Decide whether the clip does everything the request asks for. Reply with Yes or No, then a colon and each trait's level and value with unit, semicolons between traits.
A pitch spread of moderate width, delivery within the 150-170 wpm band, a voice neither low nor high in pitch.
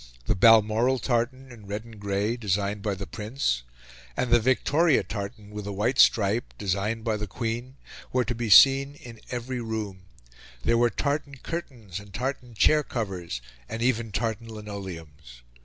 No: average, 3.4 semitones; average, 160 wpm; low, 110 Hz